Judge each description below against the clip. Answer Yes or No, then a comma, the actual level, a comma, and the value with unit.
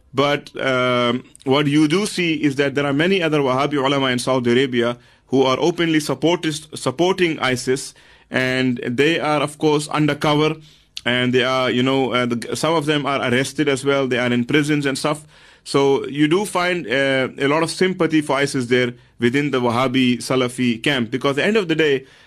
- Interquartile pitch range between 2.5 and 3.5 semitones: Yes, average, 3.0 semitones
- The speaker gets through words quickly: No, average, 195 wpm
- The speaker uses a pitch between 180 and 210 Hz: No, medium, 140 Hz